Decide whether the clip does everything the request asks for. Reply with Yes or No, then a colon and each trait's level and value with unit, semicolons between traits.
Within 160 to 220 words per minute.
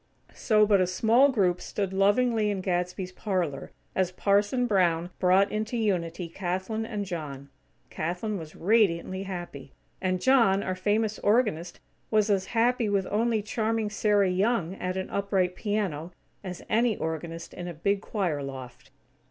No: average, 150 wpm